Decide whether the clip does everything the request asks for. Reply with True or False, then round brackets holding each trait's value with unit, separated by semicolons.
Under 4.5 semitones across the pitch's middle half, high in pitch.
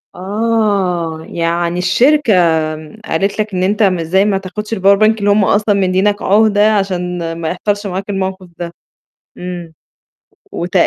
True (2.6 semitones; 195 Hz)